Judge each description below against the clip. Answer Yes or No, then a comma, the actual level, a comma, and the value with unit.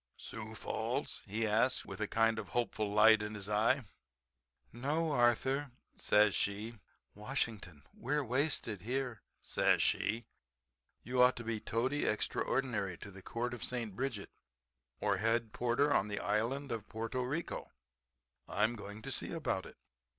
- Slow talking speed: No, average, 150 wpm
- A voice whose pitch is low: Yes, low, 115 Hz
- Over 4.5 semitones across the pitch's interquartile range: No, average, 3.2 semitones